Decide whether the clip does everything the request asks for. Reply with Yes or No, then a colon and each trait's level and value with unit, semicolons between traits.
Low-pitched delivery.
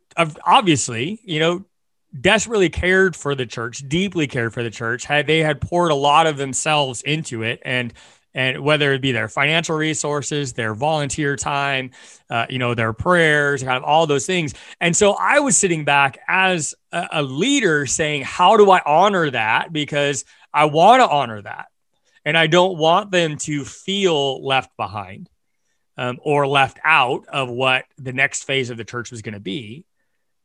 No: medium, 145 Hz